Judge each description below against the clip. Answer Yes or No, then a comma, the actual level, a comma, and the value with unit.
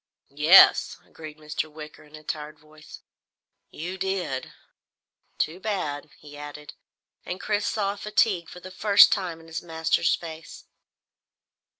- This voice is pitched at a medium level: Yes, medium, 160 Hz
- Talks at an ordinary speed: No, slow, 130 wpm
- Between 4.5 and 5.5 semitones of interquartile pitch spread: No, average, 3.6 semitones